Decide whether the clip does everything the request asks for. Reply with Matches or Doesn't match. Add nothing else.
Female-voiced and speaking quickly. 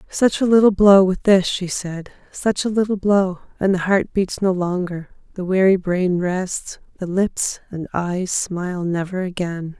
Doesn't match